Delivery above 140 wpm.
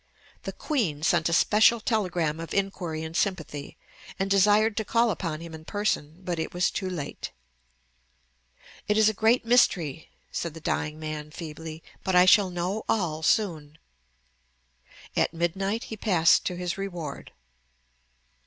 Yes: average, 150 wpm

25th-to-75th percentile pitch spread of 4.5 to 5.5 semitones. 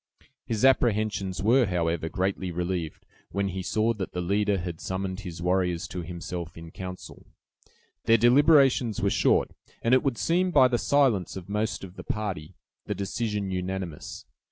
No: average, 4.1 semitones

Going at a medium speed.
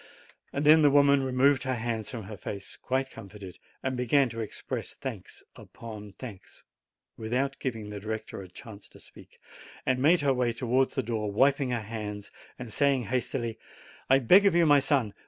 Yes: average, 175 wpm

